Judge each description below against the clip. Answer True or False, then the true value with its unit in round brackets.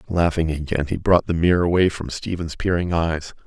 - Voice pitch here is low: True (85 Hz)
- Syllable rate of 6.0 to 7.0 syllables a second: False (5.4 syllables/s)